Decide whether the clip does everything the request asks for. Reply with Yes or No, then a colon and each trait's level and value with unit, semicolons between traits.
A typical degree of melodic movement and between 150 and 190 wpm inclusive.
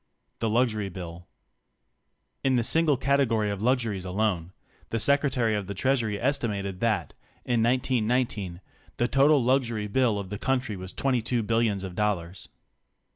No: average, 4.2 semitones; average, 140 wpm